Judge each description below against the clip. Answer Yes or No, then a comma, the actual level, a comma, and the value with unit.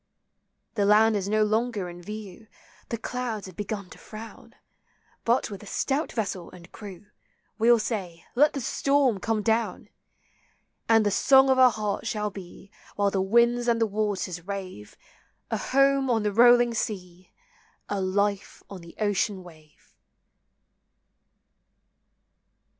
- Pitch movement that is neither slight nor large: Yes, average, 3.3 semitones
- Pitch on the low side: No, high, 210 Hz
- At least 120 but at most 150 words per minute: Yes, average, 145 wpm